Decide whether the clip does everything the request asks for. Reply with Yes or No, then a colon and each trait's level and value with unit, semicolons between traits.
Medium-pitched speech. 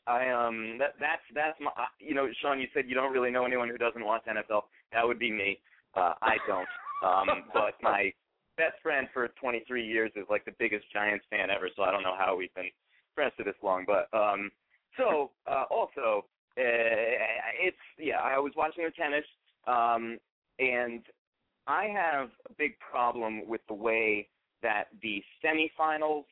No: low, 115 Hz